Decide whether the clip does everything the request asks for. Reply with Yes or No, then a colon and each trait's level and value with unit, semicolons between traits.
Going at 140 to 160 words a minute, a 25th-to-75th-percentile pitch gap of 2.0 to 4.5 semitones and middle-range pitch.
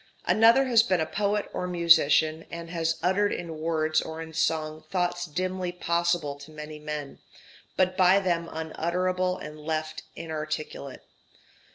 Yes: average, 145 wpm; average, 2.8 semitones; medium, 165 Hz